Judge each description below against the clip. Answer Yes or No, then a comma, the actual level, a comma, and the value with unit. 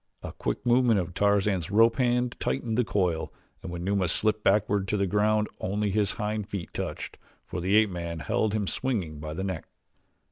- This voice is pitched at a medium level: No, low, 100 Hz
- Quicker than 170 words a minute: Yes, average, 190 wpm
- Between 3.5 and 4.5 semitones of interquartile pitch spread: No, average, 2.9 semitones